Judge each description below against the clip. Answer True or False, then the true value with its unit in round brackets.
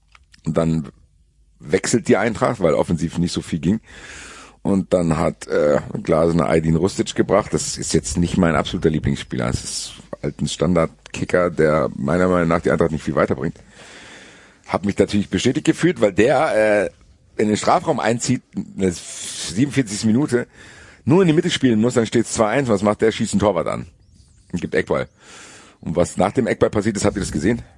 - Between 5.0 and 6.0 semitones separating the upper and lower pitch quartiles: True (5.4 semitones)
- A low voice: True (100 Hz)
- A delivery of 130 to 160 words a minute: False (185 wpm)